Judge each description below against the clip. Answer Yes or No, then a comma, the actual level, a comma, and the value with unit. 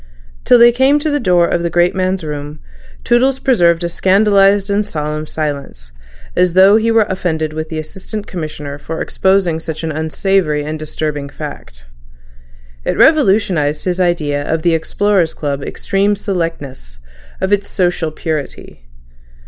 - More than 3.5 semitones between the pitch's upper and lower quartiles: Yes, average, 4.3 semitones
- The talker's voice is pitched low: No, medium, 170 Hz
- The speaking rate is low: No, average, 150 wpm